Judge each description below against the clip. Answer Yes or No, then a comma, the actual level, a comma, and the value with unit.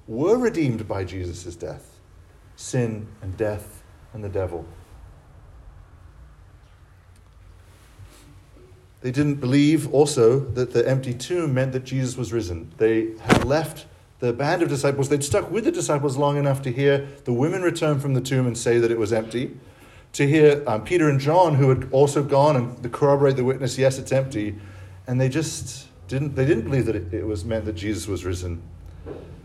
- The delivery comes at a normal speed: Yes, average, 175 wpm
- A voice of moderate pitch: No, low, 120 Hz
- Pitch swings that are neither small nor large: No, wide, 6.3 semitones